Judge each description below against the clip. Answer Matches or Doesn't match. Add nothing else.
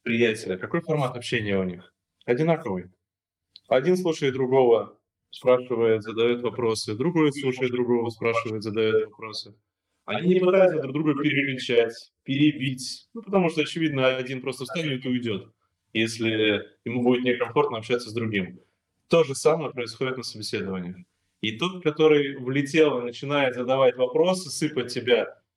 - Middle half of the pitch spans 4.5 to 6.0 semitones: Matches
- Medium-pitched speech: Doesn't match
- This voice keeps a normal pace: Matches